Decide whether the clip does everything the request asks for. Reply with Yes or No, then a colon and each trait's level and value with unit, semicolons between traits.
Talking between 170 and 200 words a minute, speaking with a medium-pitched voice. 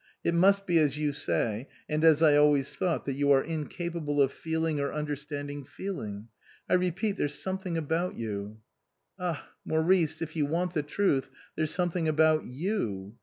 Yes: average, 180 wpm; medium, 155 Hz